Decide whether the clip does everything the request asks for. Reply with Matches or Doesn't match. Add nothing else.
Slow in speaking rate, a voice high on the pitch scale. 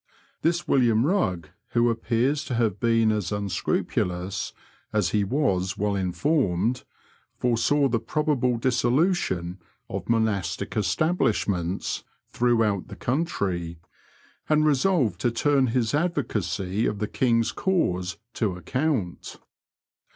Doesn't match